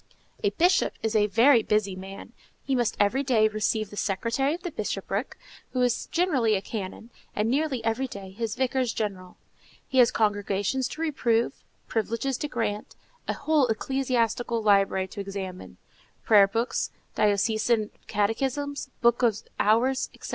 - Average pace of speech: Yes, average, 145 wpm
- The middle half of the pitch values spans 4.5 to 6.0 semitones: No, average, 4.1 semitones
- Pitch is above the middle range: Yes, high, 225 Hz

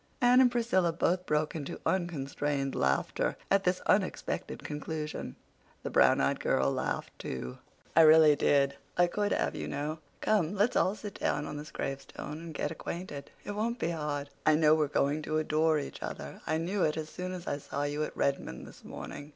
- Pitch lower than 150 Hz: No, medium, 155 Hz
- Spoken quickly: No, average, 190 wpm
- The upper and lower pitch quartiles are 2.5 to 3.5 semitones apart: No, average, 3.9 semitones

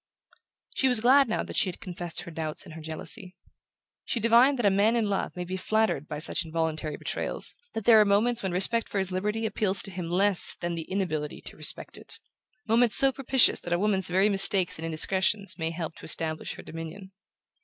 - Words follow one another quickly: Yes, fast, 210 wpm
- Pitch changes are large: No, average, 4.6 semitones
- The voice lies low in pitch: No, high, 190 Hz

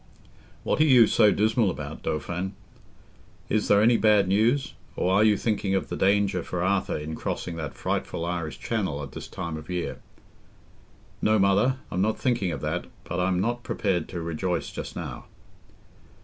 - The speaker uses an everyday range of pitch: Yes, average, 3.6 semitones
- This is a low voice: Yes, very low, 95 Hz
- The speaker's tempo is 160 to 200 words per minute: Yes, average, 175 wpm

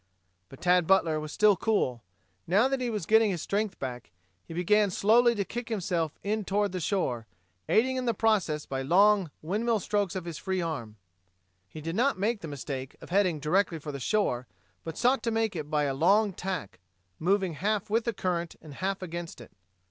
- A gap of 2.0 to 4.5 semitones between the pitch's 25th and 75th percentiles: No, average, 5.2 semitones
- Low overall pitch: No, high, 190 Hz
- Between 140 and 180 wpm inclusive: No, average, 195 wpm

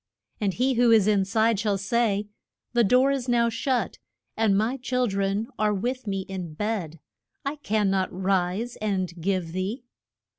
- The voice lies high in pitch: Yes, high, 210 Hz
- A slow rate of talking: No, average, 170 wpm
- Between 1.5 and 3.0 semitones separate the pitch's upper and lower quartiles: No, average, 3.7 semitones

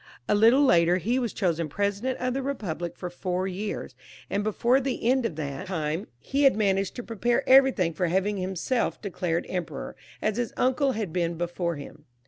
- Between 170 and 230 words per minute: Yes, average, 185 wpm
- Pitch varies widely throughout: Yes, wide, 5.9 semitones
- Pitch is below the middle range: No, high, 195 Hz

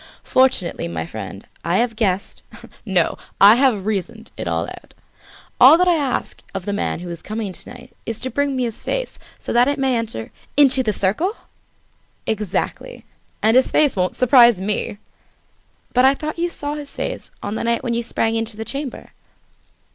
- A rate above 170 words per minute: Yes, average, 190 wpm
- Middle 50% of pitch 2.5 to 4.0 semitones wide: No, average, 5.0 semitones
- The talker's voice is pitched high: Yes, high, 230 Hz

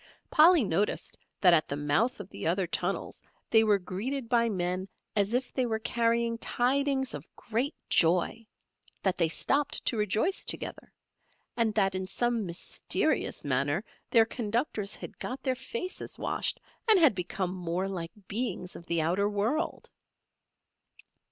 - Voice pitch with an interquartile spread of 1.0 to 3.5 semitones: No, average, 5.1 semitones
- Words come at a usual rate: Yes, average, 150 wpm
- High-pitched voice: Yes, high, 210 Hz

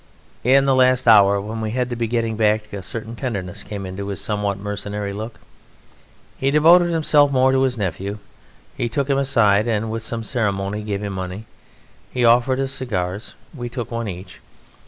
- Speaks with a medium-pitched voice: No, low, 110 Hz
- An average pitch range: Yes, average, 4.0 semitones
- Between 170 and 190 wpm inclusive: Yes, average, 185 wpm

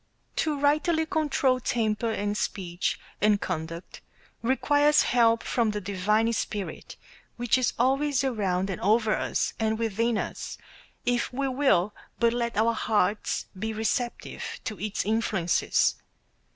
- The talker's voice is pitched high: Yes, high, 225 Hz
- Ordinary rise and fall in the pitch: Yes, average, 3.5 semitones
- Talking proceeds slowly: Yes, slow, 130 wpm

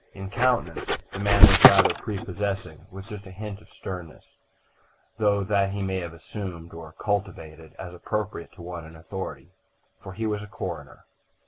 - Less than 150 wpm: No, average, 165 wpm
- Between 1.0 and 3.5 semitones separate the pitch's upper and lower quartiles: Yes, average, 3.0 semitones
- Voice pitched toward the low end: Yes, very low, 95 Hz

